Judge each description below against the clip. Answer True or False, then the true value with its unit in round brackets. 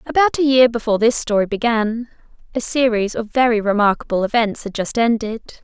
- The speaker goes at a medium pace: True (170 wpm)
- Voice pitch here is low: False (230 Hz)